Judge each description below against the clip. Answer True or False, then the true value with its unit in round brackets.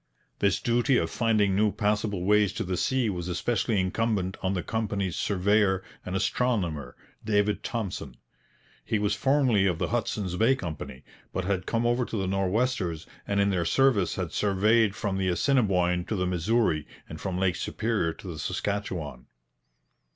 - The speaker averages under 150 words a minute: False (165 wpm)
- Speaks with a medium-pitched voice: False (100 Hz)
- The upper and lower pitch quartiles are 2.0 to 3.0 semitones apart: False (3.6 semitones)